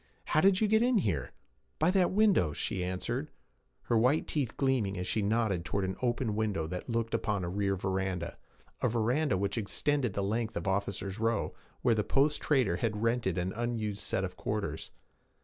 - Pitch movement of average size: Yes, average, 4.7 semitones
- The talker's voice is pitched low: Yes, low, 110 Hz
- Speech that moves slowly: No, average, 185 wpm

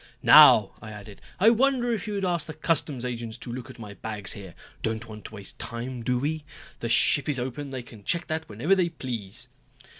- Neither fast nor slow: No, fast, 215 wpm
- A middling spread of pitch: No, wide, 6.2 semitones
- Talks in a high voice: No, low, 125 Hz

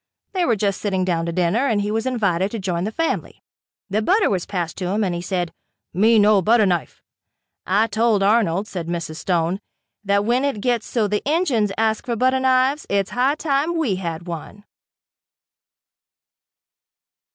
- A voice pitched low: No, high, 210 Hz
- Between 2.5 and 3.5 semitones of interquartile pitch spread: No, average, 4.6 semitones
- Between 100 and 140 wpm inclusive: No, average, 175 wpm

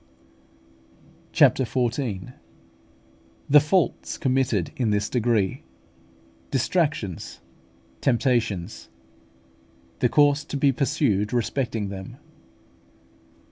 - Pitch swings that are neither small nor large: Yes, average, 4.9 semitones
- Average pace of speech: No, slow, 75 wpm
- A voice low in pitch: Yes, low, 120 Hz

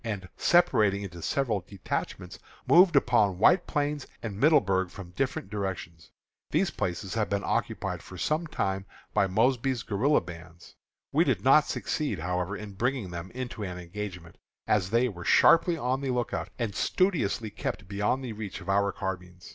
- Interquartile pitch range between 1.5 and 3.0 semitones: No, wide, 5.4 semitones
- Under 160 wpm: No, average, 165 wpm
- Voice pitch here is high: No, low, 100 Hz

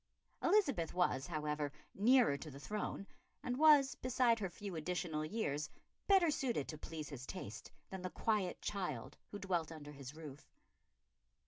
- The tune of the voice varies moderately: No, wide, 6.9 semitones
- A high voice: No, medium, 180 Hz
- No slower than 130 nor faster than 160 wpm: Yes, average, 150 wpm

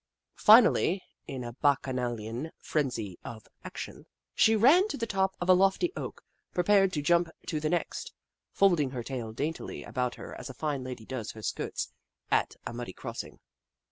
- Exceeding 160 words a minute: Yes, average, 175 wpm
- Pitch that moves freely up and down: Yes, wide, 7.5 semitones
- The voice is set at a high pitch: No, medium, 145 Hz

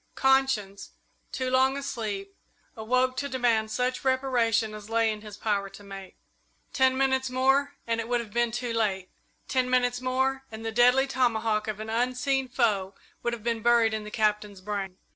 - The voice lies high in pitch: Yes, high, 235 Hz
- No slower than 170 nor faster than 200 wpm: Yes, average, 180 wpm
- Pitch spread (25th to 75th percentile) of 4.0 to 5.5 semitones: No, average, 3.3 semitones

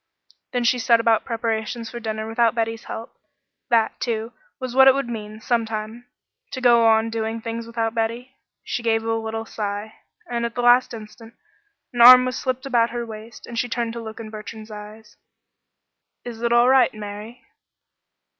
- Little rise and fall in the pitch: Yes, narrow, 1.4 semitones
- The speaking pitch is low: No, high, 230 Hz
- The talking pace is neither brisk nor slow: Yes, average, 175 wpm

